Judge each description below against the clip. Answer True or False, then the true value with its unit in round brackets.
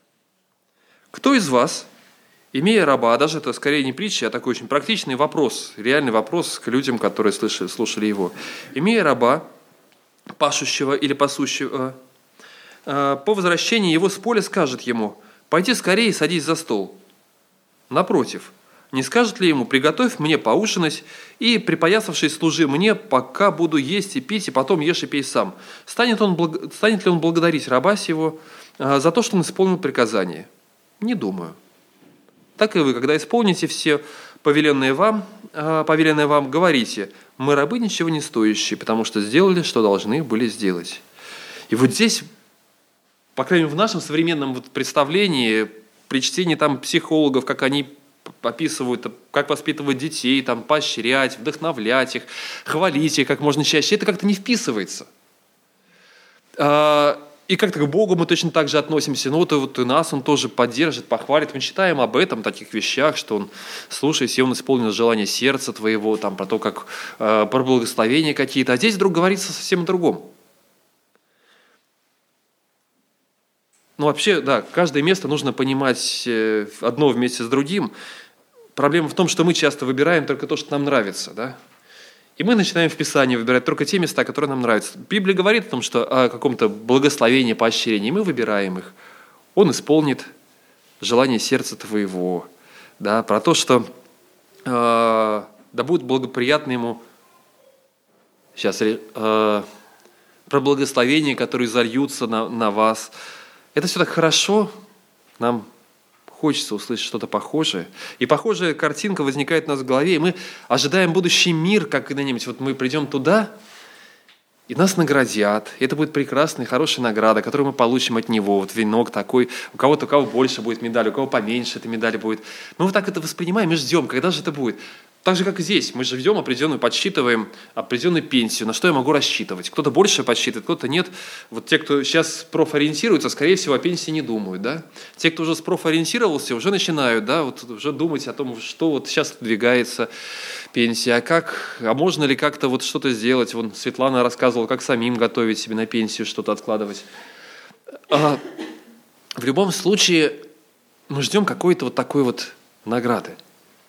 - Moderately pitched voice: True (145 Hz)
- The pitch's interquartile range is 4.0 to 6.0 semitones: True (5.5 semitones)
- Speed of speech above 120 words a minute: True (160 wpm)